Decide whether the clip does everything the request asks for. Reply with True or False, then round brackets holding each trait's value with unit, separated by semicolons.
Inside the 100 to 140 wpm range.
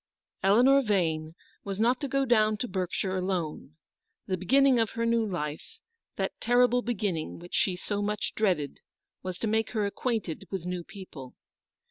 False (160 wpm)